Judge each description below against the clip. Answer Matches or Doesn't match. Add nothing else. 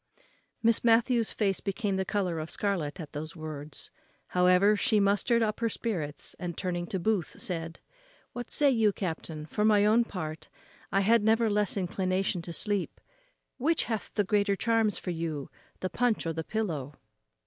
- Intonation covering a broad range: Doesn't match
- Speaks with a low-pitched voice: Doesn't match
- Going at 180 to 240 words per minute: Doesn't match